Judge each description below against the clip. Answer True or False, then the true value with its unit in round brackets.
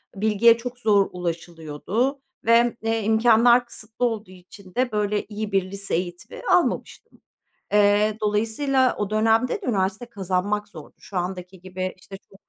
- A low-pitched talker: False (210 Hz)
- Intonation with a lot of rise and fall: False (3.3 semitones)